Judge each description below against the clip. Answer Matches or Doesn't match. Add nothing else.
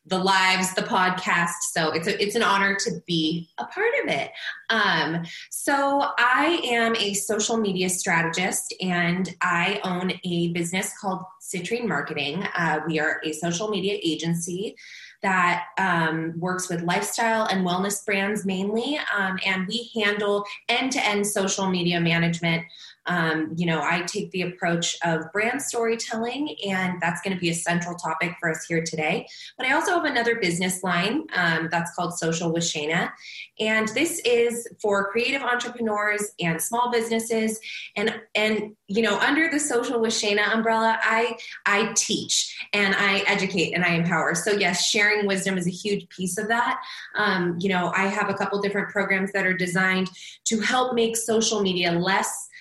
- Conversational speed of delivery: Matches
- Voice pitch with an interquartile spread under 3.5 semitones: Doesn't match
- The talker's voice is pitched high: Matches